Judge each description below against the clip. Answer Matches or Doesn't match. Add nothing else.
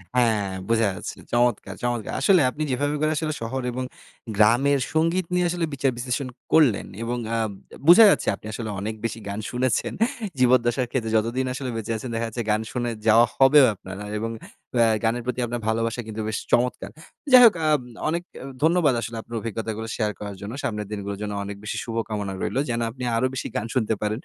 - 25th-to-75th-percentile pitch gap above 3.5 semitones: Doesn't match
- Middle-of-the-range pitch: Doesn't match